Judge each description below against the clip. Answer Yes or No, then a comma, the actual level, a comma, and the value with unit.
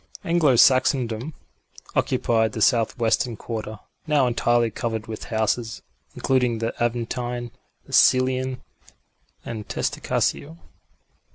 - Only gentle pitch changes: Yes, narrow, 2.3 semitones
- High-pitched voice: No, low, 120 Hz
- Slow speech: Yes, slow, 95 wpm